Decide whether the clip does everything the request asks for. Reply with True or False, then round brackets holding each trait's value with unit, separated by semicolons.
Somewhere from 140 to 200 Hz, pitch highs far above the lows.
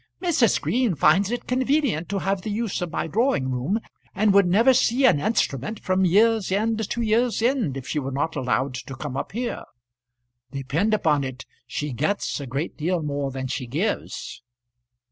True (185 Hz; 8.2 semitones)